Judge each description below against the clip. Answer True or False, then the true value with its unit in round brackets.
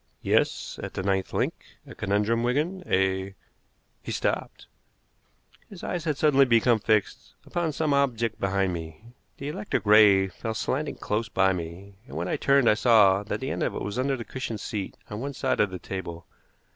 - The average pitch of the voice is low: True (110 Hz)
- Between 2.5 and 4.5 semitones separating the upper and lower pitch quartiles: False (5.5 semitones)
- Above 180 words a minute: True (190 wpm)